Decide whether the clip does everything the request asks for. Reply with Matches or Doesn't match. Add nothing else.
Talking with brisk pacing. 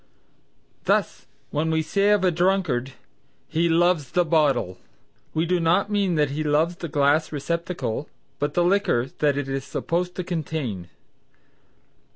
Doesn't match